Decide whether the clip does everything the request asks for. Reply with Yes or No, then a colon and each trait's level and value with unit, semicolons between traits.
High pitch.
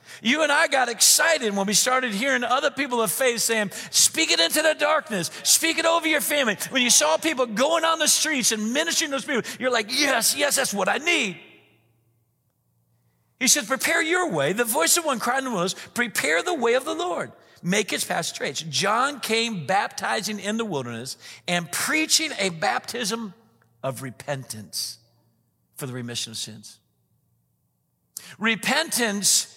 Yes: high, 225 Hz